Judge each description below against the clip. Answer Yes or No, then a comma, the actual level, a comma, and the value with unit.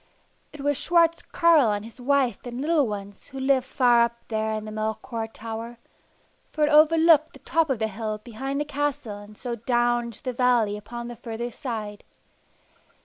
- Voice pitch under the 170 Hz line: No, high, 240 Hz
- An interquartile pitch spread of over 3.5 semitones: Yes, average, 4.3 semitones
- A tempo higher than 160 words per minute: Yes, average, 185 wpm